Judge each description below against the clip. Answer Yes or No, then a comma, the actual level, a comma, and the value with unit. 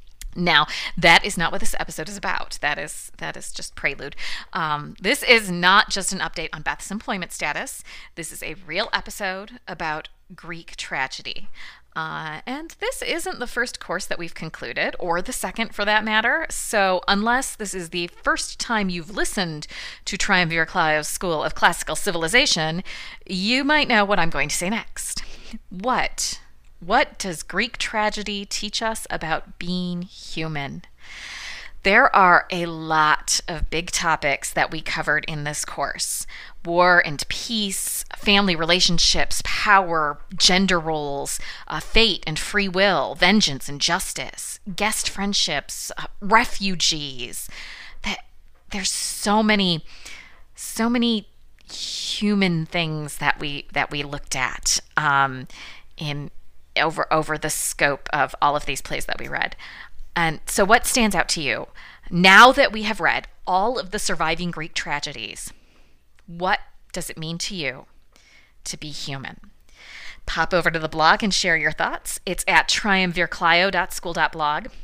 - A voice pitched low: No, medium, 180 Hz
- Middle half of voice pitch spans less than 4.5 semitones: No, average, 5.1 semitones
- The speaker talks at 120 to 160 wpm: Yes, average, 150 wpm